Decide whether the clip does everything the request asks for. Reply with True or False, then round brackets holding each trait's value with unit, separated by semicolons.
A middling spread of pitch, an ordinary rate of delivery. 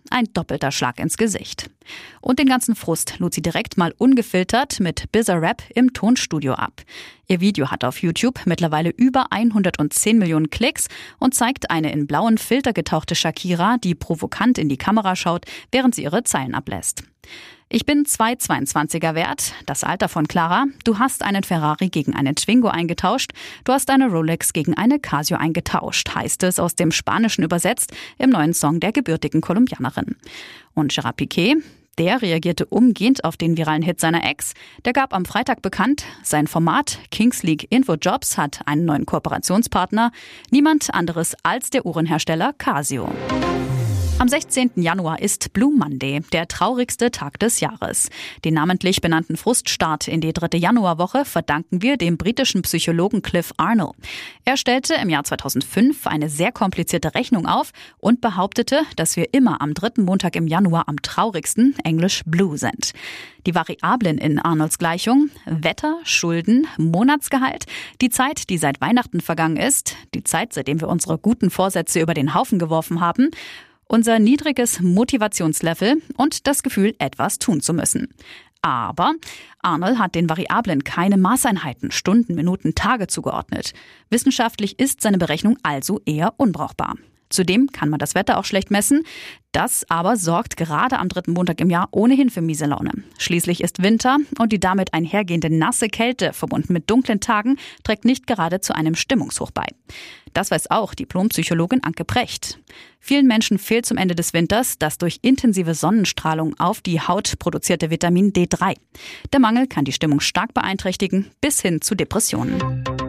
False (6.6 semitones; 160 wpm)